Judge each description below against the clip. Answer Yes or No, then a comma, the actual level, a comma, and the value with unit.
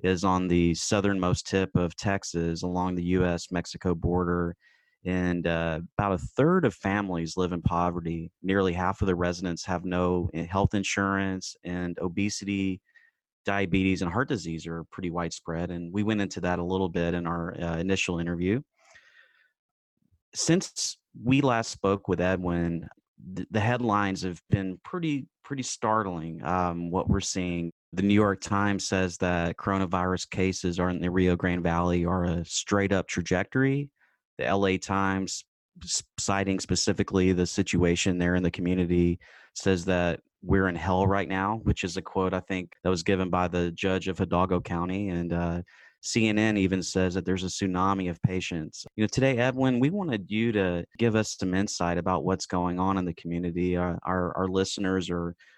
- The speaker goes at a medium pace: Yes, average, 170 wpm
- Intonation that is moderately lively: No, narrow, 2.0 semitones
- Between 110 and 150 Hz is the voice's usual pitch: No, very low, 95 Hz